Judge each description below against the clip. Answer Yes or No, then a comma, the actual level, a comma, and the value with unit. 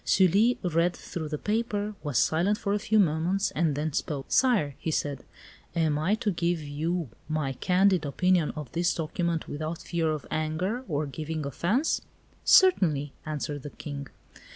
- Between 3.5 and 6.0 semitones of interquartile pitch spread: Yes, average, 4.0 semitones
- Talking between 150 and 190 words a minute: Yes, average, 160 wpm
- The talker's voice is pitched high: No, medium, 165 Hz